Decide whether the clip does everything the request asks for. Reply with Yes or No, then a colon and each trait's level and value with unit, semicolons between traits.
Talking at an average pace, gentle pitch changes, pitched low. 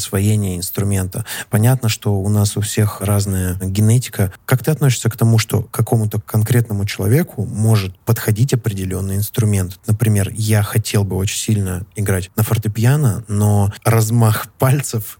Yes: average, 140 wpm; narrow, 2.3 semitones; low, 110 Hz